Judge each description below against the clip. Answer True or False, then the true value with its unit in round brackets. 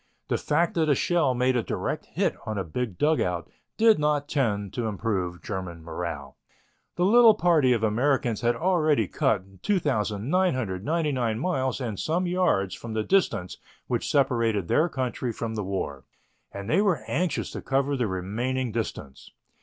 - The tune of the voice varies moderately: False (7.0 semitones)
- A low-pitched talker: True (125 Hz)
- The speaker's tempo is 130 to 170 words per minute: True (160 wpm)